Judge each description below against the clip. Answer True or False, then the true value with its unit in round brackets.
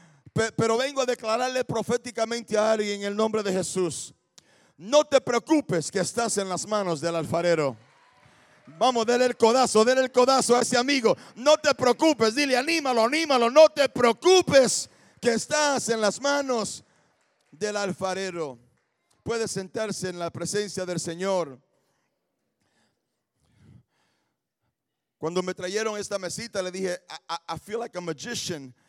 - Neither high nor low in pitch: False (220 Hz)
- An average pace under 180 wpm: True (145 wpm)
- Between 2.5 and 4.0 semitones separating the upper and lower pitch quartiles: False (5.2 semitones)